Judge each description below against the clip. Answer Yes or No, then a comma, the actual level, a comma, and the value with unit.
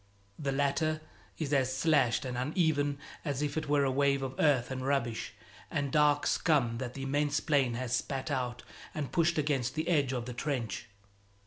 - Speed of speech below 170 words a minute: No, average, 185 wpm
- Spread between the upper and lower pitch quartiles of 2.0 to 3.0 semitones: Yes, narrow, 2.4 semitones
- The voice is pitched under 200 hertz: Yes, medium, 140 Hz